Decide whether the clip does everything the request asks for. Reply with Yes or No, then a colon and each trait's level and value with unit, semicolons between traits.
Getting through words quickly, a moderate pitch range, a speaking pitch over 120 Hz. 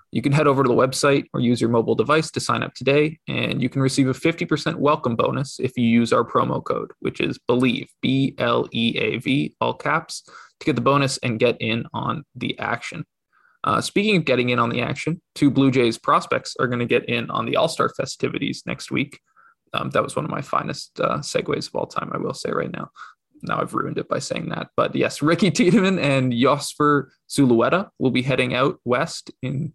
Yes: fast, 220 wpm; average, 3.4 semitones; low, 130 Hz